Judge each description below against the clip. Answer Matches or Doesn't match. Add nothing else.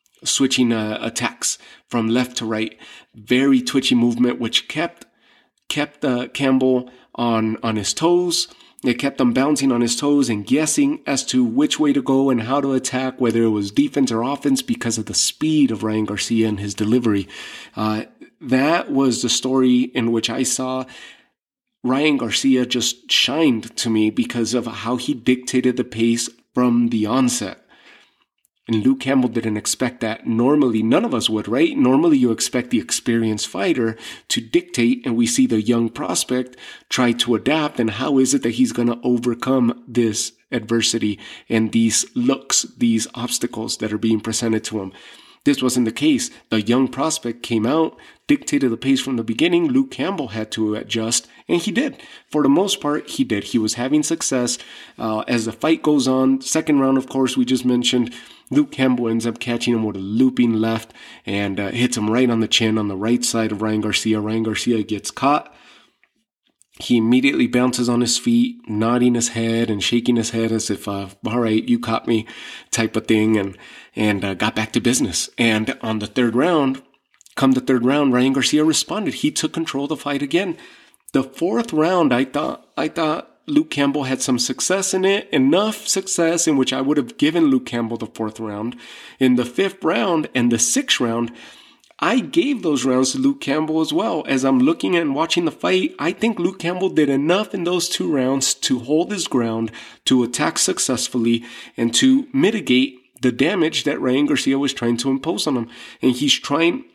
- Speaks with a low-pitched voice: Matches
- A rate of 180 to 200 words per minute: Matches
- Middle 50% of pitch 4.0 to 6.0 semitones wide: Matches